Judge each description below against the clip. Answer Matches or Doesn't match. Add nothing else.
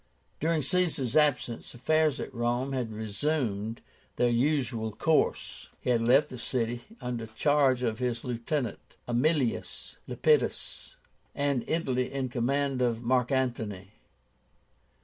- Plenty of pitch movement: Doesn't match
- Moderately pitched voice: Doesn't match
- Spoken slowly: Matches